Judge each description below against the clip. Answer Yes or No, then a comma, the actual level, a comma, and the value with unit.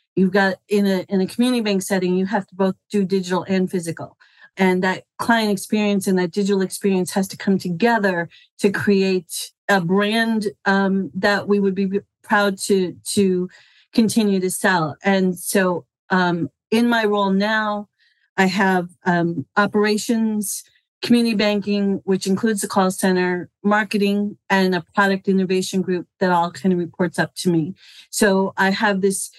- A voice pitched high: Yes, high, 195 Hz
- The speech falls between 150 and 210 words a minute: Yes, average, 165 wpm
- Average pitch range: No, narrow, 1.8 semitones